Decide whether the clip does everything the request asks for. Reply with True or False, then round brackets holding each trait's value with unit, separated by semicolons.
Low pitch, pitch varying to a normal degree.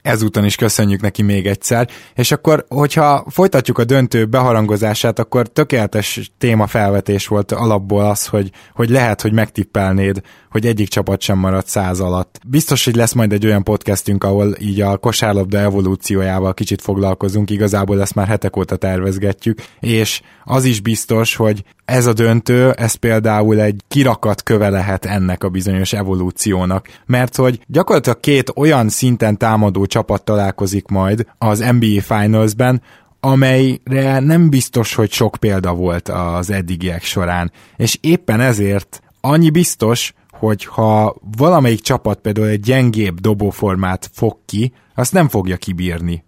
True (105 Hz; 3.4 semitones)